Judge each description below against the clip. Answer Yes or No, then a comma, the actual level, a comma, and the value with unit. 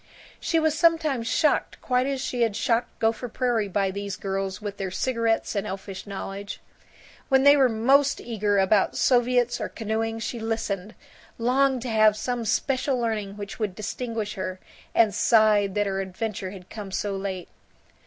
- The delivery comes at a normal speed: Yes, average, 165 wpm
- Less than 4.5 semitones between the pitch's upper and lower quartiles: Yes, average, 3.7 semitones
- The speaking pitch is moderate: No, high, 220 Hz